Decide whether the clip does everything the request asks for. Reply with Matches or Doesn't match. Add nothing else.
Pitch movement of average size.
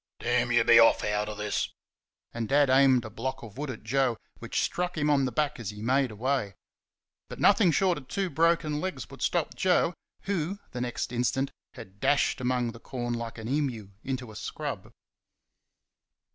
Matches